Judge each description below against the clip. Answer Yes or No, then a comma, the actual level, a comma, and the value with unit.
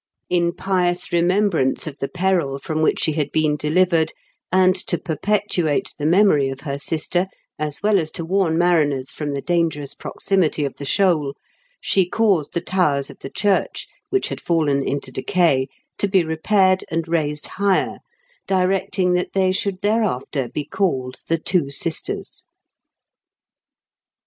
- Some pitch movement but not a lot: Yes, average, 4.2 semitones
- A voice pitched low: No, medium, 170 Hz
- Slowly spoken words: No, average, 150 wpm